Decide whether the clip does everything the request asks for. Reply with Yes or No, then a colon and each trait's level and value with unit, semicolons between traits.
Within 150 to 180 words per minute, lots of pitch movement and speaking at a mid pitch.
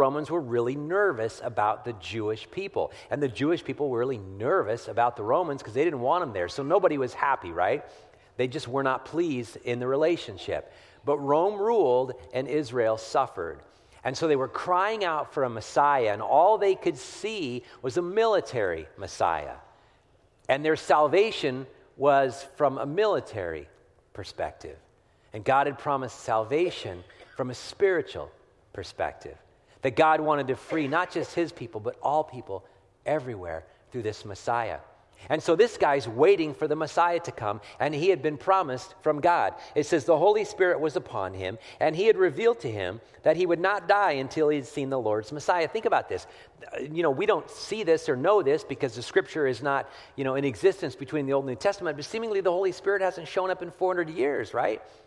No: average, 190 wpm; wide, 6.8 semitones; medium, 145 Hz